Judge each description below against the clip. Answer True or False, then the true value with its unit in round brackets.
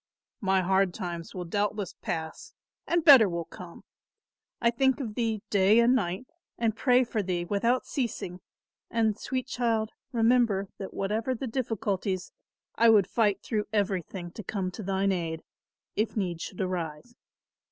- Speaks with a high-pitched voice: True (205 Hz)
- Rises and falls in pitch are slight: False (4.0 semitones)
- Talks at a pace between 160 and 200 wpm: False (150 wpm)